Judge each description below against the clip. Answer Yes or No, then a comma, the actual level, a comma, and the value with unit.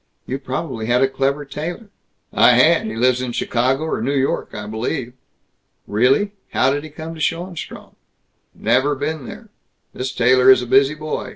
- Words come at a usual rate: Yes, average, 175 wpm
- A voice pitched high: No, low, 135 Hz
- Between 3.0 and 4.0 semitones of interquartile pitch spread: Yes, average, 3.4 semitones